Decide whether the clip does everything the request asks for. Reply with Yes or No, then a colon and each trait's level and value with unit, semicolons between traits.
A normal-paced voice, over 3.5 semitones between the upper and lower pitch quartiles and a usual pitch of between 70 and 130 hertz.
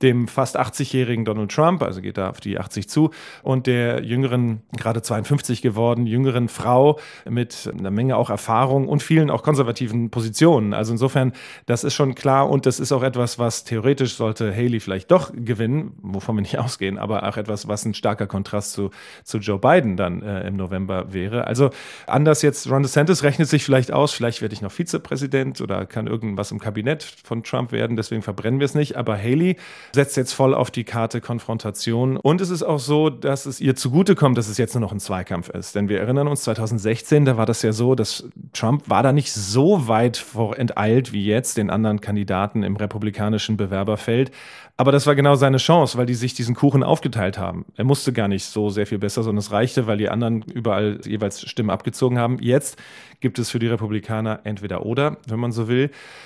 No: fast, 205 wpm; average, 4.1 semitones; low, 120 Hz